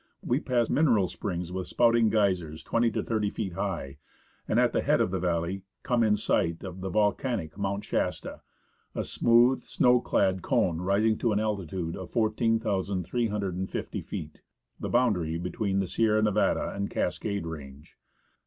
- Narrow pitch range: No, average, 3.9 semitones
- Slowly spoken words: No, average, 160 wpm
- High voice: No, low, 100 Hz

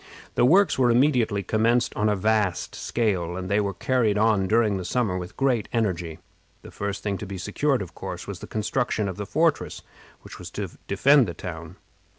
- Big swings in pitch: No, average, 4.3 semitones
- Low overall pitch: Yes, low, 105 Hz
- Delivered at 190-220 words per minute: Yes, average, 195 wpm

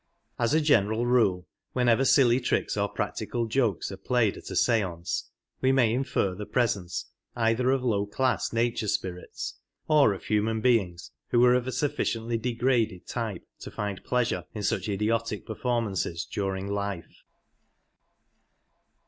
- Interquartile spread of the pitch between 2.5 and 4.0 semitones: Yes, average, 3.6 semitones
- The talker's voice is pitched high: No, low, 115 Hz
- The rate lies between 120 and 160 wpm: Yes, average, 150 wpm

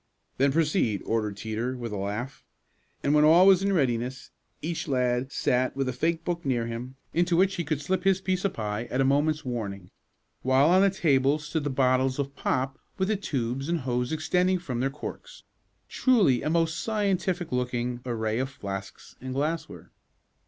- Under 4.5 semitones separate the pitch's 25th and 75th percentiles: No, wide, 5.4 semitones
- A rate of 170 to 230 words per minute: Yes, average, 185 wpm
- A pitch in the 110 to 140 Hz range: Yes, low, 135 Hz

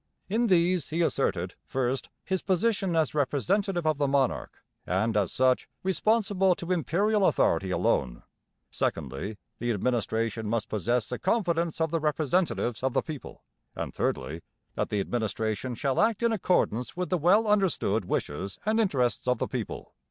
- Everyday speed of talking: Yes, average, 155 wpm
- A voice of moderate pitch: Yes, medium, 145 Hz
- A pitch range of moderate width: No, wide, 8.5 semitones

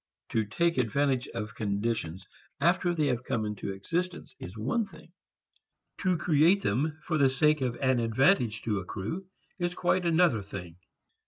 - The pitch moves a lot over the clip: Yes, wide, 7.9 semitones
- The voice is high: No, low, 130 Hz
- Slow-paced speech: No, average, 155 wpm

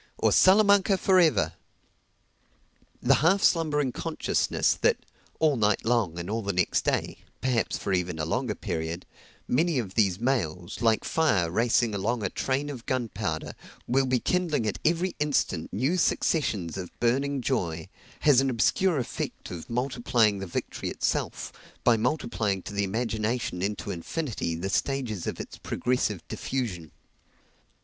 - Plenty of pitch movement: Yes, wide, 6.2 semitones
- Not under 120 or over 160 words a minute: Yes, average, 145 wpm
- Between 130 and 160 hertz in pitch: No, low, 115 Hz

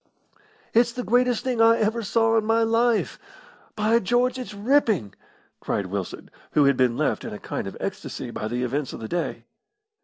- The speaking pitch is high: Yes, high, 225 Hz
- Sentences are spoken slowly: No, average, 185 wpm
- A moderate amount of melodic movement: No, wide, 9.0 semitones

